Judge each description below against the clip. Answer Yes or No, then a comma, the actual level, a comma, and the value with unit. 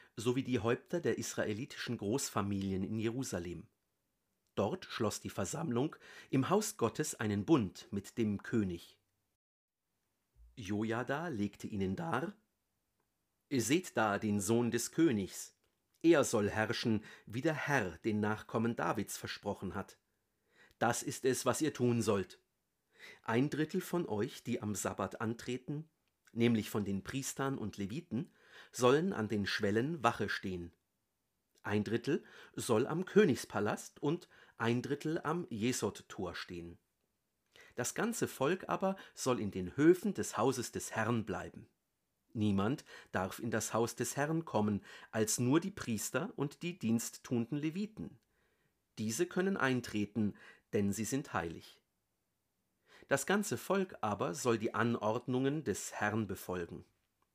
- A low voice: Yes, low, 115 Hz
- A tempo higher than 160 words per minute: No, average, 130 wpm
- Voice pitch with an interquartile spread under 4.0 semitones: No, average, 4.6 semitones